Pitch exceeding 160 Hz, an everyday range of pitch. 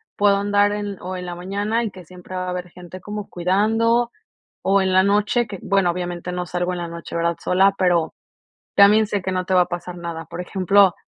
No: medium, 185 Hz; narrow, 2.3 semitones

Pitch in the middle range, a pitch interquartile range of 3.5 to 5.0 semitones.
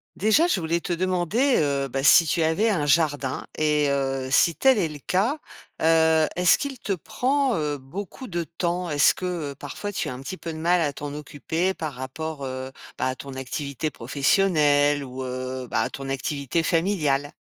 Yes: medium, 155 Hz; average, 4.4 semitones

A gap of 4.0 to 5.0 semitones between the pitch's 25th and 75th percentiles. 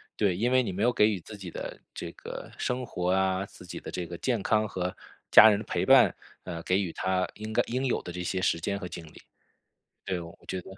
No: average, 3.2 semitones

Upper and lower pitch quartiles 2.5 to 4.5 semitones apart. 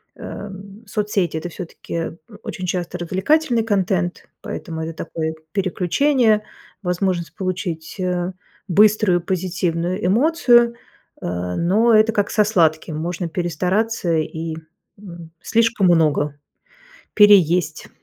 Yes: average, 3.8 semitones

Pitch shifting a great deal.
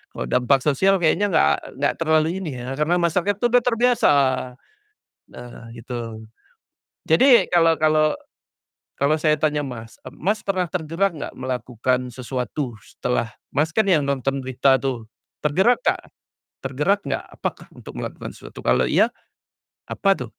Yes: wide, 5.8 semitones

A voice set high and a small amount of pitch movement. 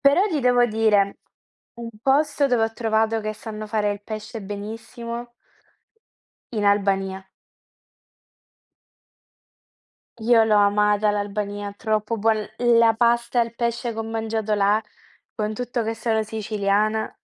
Yes: high, 220 Hz; narrow, 2.0 semitones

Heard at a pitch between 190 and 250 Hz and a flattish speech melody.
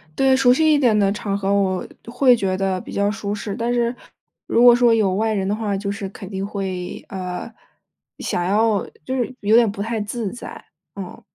No: high, 210 Hz; average, 3.3 semitones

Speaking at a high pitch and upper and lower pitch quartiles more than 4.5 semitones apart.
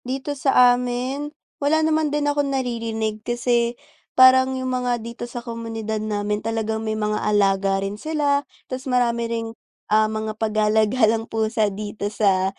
No: high, 230 Hz; average, 3.1 semitones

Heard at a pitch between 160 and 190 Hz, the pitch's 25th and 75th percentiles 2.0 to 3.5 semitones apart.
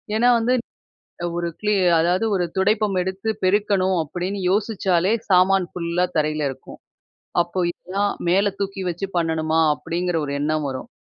Yes: medium, 185 Hz; average, 2.9 semitones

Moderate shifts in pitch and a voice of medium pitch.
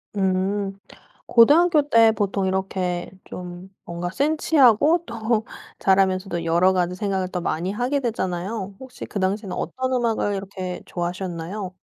No: average, 3.9 semitones; high, 195 Hz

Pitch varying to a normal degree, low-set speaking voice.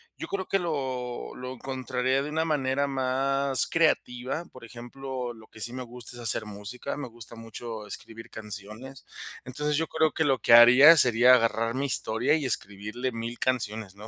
Yes: average, 3.1 semitones; low, 125 Hz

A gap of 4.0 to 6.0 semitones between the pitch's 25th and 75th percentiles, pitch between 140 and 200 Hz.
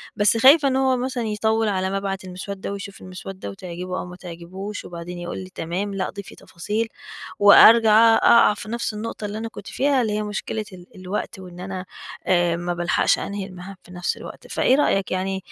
No: average, 3.1 semitones; high, 195 Hz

